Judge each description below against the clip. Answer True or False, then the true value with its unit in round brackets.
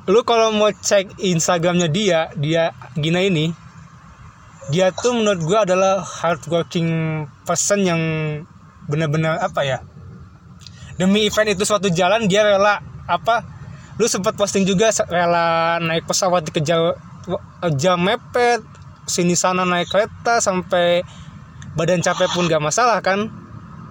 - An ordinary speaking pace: True (125 wpm)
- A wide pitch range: False (3.8 semitones)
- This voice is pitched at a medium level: True (175 Hz)